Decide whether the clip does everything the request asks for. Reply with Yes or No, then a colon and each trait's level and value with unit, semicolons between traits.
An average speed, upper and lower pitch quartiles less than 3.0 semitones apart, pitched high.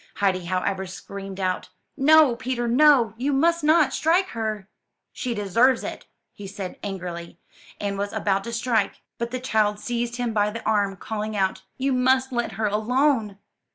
No: average, 165 wpm; average, 4.5 semitones; high, 225 Hz